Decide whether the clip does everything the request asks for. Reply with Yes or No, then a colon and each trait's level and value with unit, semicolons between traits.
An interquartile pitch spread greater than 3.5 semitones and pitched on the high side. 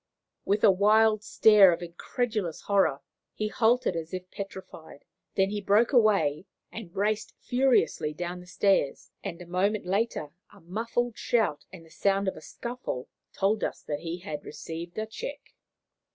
Yes: average, 4.1 semitones; high, 195 Hz